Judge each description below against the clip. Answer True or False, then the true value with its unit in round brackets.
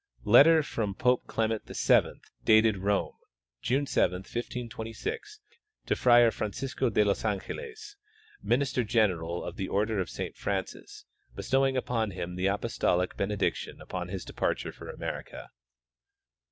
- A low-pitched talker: True (110 Hz)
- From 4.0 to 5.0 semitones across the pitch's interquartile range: True (4.6 semitones)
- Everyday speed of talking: False (130 wpm)